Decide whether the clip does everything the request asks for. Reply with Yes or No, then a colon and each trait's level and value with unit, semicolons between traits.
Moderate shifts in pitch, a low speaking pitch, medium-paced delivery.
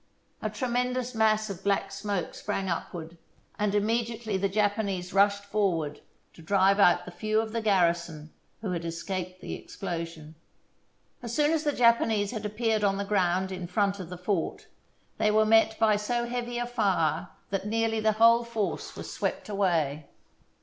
No: average, 3.5 semitones; high, 205 Hz; average, 165 wpm